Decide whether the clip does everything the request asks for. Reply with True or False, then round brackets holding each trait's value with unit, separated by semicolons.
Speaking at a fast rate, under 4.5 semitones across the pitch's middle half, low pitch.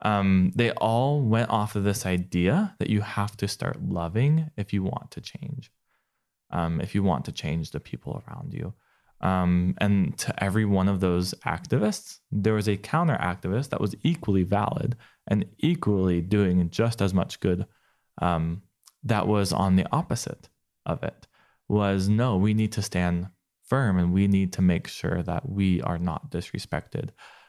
False (170 wpm; 3.0 semitones; 100 Hz)